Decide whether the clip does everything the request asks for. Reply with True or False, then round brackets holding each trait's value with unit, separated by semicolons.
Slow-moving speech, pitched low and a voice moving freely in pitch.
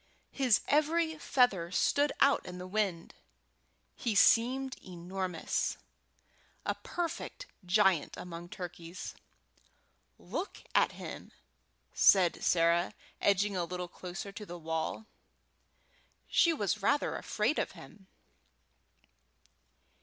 False (100 wpm; 195 Hz; 6.3 semitones)